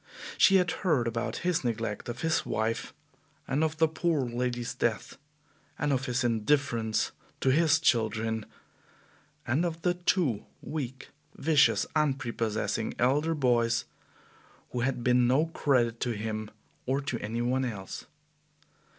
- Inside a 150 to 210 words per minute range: No, slow, 135 wpm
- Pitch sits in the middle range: No, low, 125 Hz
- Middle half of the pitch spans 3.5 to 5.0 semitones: Yes, average, 4.6 semitones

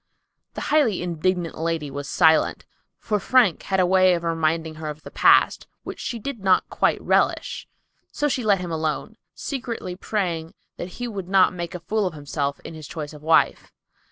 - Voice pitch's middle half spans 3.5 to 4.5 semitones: Yes, average, 3.9 semitones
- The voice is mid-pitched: Yes, medium, 175 Hz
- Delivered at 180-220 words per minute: Yes, average, 190 wpm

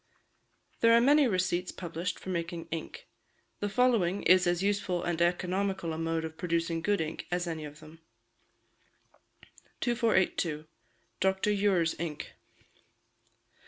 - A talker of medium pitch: Yes, medium, 180 Hz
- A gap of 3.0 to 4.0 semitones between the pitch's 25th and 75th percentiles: Yes, average, 3.3 semitones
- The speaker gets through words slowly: Yes, slow, 125 wpm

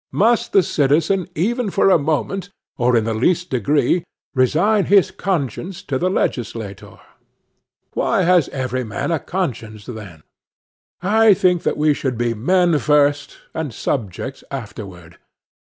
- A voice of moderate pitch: Yes, medium, 145 Hz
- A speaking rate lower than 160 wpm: Yes, average, 140 wpm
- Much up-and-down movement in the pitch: Yes, wide, 7.2 semitones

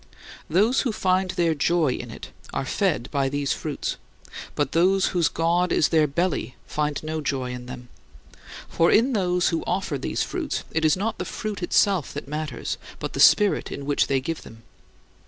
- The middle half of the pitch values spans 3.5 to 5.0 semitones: Yes, average, 4.5 semitones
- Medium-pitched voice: Yes, medium, 165 Hz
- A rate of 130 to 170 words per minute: No, average, 185 wpm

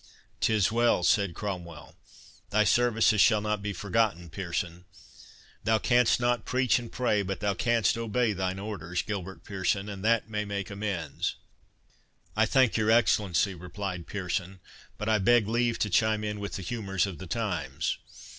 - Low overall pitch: Yes, low, 105 Hz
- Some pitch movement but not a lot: Yes, average, 3.1 semitones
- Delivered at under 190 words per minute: Yes, average, 160 wpm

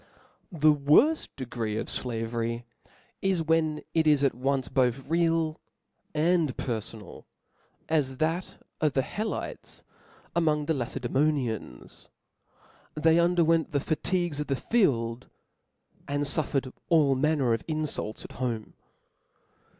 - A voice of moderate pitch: Yes, medium, 145 Hz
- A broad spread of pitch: No, average, 4.3 semitones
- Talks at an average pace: No, slow, 120 wpm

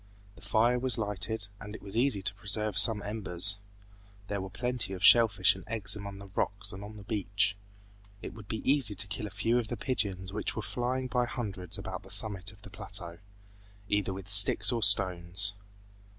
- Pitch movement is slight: Yes, narrow, 2.3 semitones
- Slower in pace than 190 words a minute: No, average, 200 wpm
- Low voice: Yes, low, 105 Hz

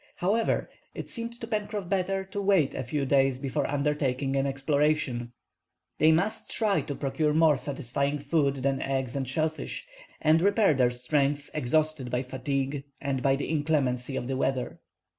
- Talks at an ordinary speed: Yes, average, 160 wpm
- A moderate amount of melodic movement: Yes, average, 3.0 semitones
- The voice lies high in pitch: No, medium, 145 Hz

